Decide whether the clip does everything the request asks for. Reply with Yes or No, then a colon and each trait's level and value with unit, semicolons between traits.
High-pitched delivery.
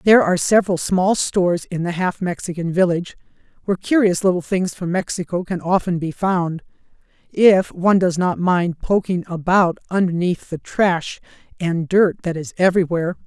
No: medium, 180 Hz